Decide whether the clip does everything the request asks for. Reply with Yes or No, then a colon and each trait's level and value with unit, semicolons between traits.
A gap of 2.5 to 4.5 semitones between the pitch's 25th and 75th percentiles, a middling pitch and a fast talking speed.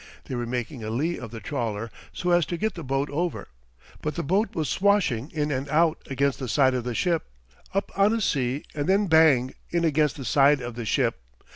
No: average, 5.3 semitones; medium, 145 Hz; fast, 225 wpm